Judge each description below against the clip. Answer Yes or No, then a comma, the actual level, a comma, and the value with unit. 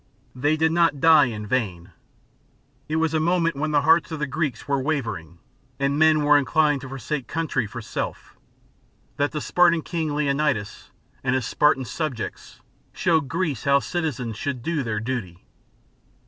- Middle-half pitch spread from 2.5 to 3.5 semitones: No, average, 4.0 semitones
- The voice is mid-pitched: Yes, medium, 145 Hz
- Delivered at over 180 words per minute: No, average, 160 wpm